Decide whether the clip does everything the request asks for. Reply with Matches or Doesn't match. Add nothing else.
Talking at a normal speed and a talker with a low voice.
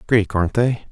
Matches